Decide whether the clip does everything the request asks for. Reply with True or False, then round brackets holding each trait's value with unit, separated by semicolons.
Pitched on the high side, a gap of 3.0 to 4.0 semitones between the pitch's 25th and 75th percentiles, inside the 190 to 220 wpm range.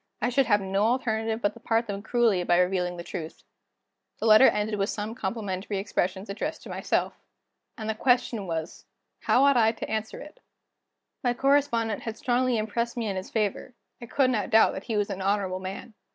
True (220 Hz; 3.3 semitones; 195 wpm)